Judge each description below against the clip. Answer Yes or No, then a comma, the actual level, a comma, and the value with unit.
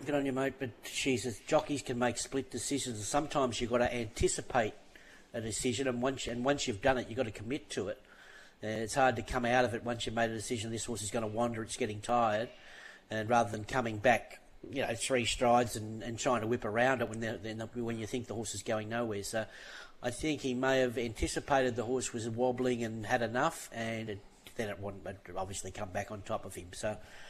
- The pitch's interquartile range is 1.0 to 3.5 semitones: Yes, narrow, 2.6 semitones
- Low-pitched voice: Yes, low, 120 Hz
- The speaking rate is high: Yes, fast, 235 wpm